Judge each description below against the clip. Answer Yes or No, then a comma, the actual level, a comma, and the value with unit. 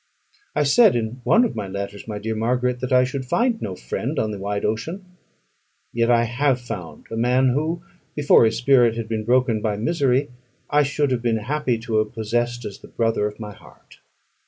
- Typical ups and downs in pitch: Yes, average, 3.3 semitones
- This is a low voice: Yes, low, 120 Hz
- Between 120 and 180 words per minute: No, fast, 205 wpm